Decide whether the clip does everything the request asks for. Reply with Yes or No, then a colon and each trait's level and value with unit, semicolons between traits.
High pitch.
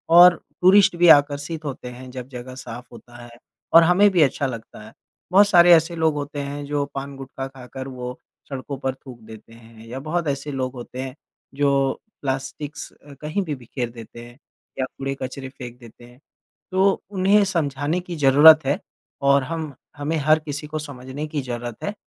No: medium, 140 Hz